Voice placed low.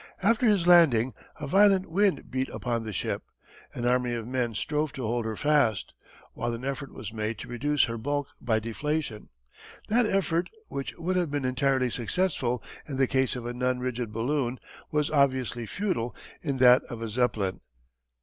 Yes: low, 130 Hz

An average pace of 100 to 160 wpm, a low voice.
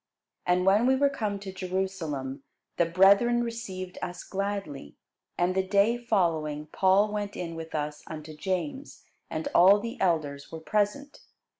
No: average, 150 wpm; high, 190 Hz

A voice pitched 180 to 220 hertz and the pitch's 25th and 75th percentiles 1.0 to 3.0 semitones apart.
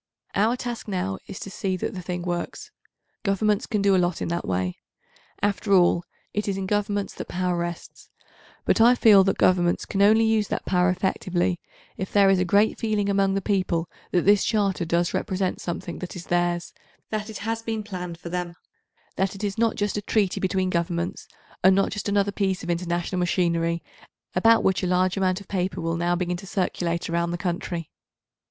Yes: medium, 185 Hz; narrow, 2.6 semitones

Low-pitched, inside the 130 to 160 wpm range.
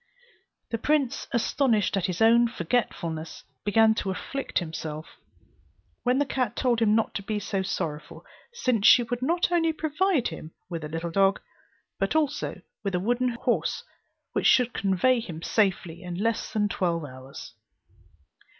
No: high, 215 Hz; average, 155 wpm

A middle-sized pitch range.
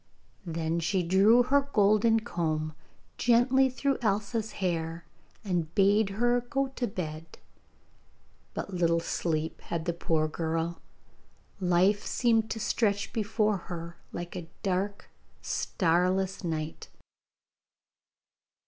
Yes: average, 4.8 semitones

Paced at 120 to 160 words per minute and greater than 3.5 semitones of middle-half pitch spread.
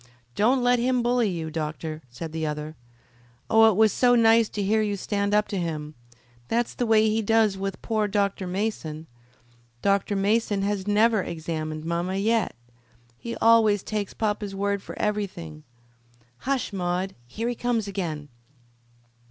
Yes: average, 155 wpm; average, 4.3 semitones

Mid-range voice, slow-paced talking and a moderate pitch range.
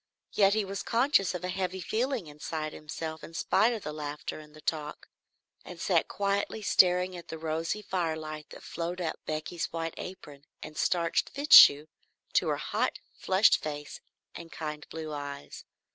No: medium, 165 Hz; average, 165 wpm; average, 3.6 semitones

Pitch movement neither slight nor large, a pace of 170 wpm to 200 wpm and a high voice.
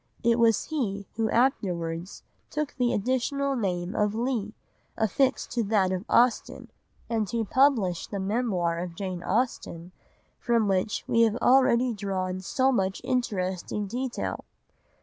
No: average, 4.7 semitones; slow, 135 wpm; high, 220 Hz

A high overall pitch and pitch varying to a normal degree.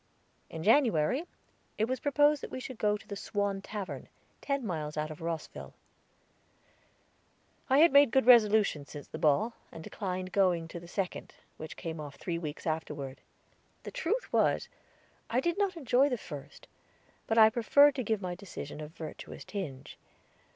No: high, 200 Hz; wide, 7.8 semitones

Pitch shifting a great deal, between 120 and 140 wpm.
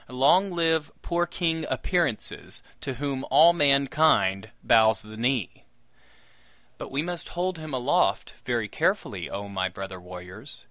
Yes: wide, 7.3 semitones; slow, 135 wpm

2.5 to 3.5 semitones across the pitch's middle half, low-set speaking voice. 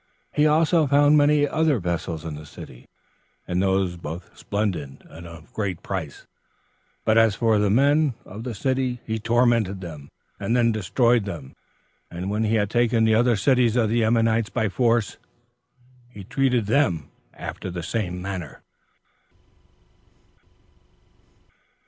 No: average, 5.1 semitones; low, 110 Hz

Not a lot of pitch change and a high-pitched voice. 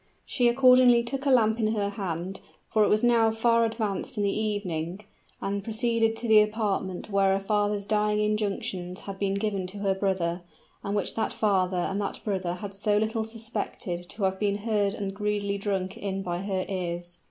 Yes: narrow, 2.2 semitones; high, 205 Hz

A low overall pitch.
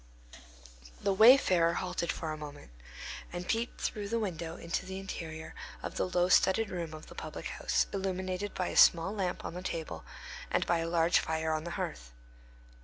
No: medium, 175 Hz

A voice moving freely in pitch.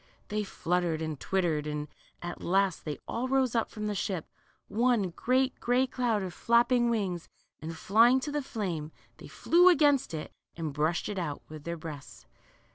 Yes: wide, 6.9 semitones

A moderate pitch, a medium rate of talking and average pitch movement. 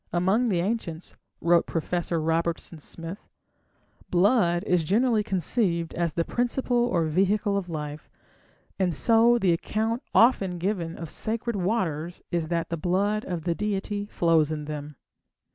Yes: medium, 180 Hz; average, 145 wpm; average, 4.1 semitones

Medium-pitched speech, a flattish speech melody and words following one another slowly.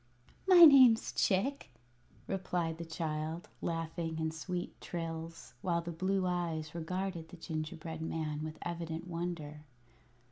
Yes: medium, 165 Hz; narrow, 2.0 semitones; slow, 120 wpm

